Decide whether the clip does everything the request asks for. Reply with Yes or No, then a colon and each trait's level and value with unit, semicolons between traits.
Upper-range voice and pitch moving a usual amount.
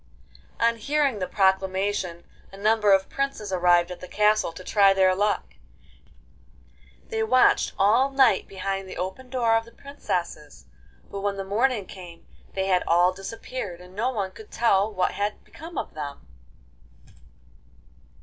Yes: high, 195 Hz; average, 3.5 semitones